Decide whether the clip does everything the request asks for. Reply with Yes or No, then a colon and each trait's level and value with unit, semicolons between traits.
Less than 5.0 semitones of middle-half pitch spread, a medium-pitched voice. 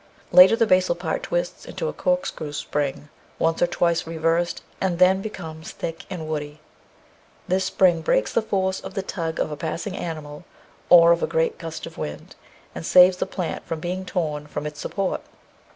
Yes: average, 3.1 semitones; medium, 170 Hz